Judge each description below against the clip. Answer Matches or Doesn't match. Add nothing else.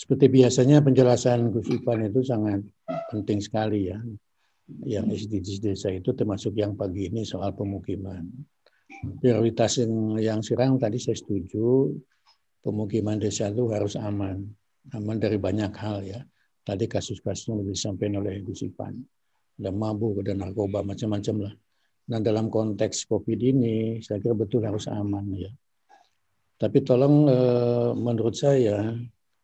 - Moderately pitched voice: Doesn't match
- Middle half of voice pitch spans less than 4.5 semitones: Matches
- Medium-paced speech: Matches